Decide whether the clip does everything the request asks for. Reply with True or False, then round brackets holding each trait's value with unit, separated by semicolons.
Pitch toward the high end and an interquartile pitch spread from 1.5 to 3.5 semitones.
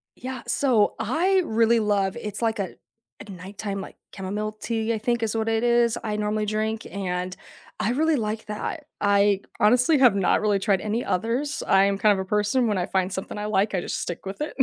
True (215 Hz; 2.7 semitones)